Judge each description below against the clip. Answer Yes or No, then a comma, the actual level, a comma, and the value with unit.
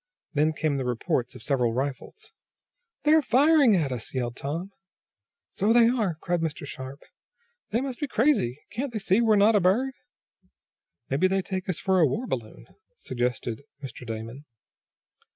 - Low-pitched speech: No, medium, 175 Hz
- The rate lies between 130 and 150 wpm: No, average, 165 wpm